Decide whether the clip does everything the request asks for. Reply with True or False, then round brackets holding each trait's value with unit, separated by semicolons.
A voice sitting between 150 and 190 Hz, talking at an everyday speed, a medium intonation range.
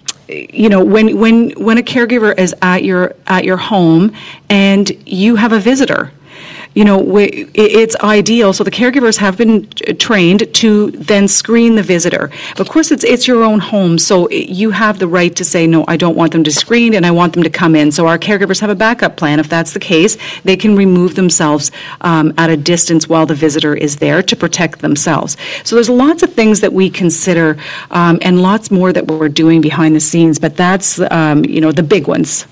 False (185 Hz; 215 wpm; 4.4 semitones)